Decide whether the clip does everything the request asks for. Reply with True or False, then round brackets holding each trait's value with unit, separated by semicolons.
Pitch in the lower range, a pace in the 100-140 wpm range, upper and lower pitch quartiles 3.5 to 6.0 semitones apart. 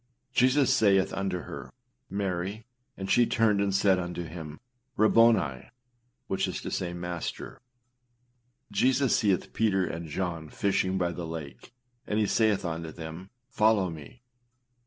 True (95 Hz; 135 wpm; 3.8 semitones)